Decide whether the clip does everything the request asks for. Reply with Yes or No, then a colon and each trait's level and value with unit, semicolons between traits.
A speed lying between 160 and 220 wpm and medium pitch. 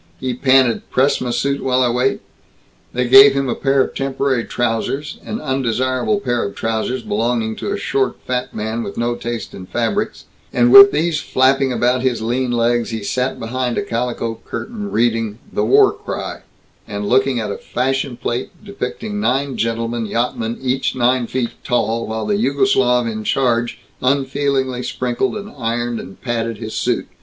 No: average, 170 wpm; low, 125 Hz